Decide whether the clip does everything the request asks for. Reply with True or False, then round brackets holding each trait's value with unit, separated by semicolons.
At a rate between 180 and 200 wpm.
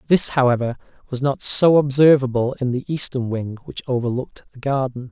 False (165 wpm)